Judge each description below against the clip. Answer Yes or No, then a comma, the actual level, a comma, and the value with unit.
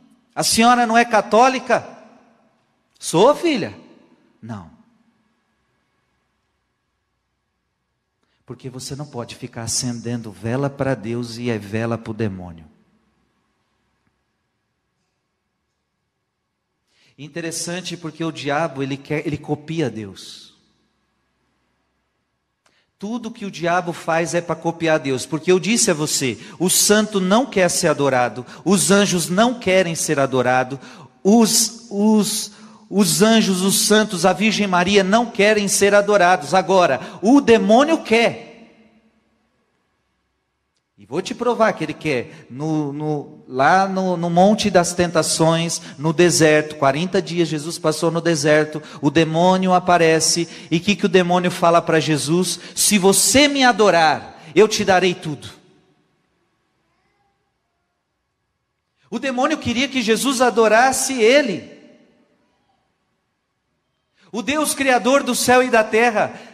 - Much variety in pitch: Yes, wide, 6.1 semitones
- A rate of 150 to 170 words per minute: No, slow, 120 wpm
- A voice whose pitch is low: No, medium, 180 Hz